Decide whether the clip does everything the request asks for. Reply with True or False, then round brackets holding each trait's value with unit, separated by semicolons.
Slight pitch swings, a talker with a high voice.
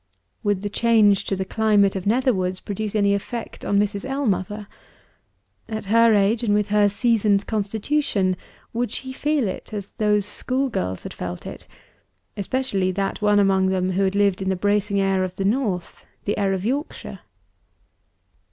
True (2.3 semitones; 205 Hz)